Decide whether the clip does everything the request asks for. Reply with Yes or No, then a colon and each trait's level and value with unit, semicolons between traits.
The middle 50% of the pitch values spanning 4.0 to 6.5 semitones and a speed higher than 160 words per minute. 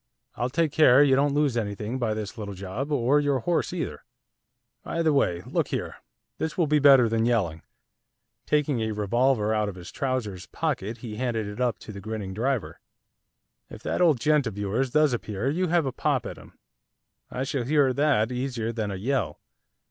Yes: average, 5.0 semitones; average, 195 wpm